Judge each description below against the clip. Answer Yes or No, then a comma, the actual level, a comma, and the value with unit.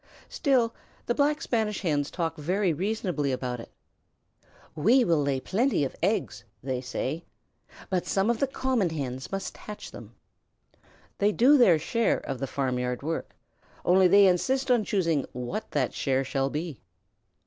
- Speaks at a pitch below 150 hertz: No, medium, 175 Hz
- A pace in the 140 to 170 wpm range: Yes, average, 155 wpm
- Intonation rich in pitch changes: Yes, wide, 8.0 semitones